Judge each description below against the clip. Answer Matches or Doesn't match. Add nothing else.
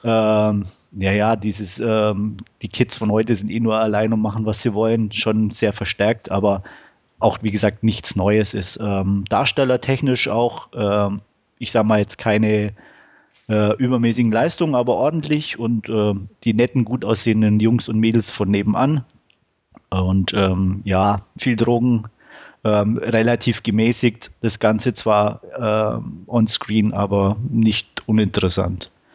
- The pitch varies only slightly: Matches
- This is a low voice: Matches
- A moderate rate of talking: Matches